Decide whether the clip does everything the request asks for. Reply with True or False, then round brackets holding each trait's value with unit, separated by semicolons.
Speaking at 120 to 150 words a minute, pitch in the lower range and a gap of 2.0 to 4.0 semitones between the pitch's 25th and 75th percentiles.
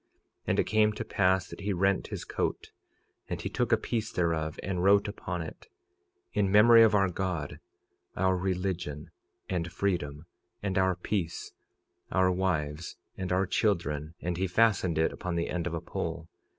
False (165 wpm; 90 Hz; 2.9 semitones)